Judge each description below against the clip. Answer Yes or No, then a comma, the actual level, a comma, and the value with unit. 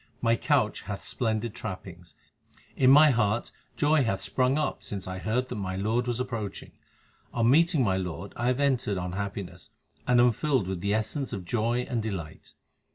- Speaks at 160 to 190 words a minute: Yes, average, 180 wpm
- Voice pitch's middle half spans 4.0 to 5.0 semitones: Yes, average, 4.6 semitones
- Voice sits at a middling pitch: No, low, 110 Hz